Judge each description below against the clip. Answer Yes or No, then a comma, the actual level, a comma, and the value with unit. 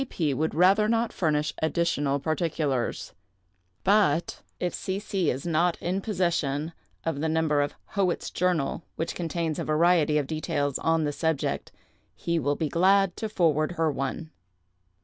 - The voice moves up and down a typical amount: Yes, average, 3.0 semitones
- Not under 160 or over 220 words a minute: No, average, 150 wpm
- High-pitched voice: No, medium, 160 Hz